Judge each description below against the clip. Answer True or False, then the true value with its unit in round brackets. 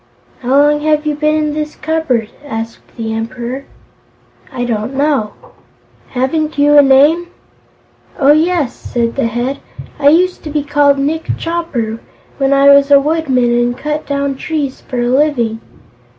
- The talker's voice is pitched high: True (280 Hz)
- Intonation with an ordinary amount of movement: True (3.7 semitones)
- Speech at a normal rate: True (155 wpm)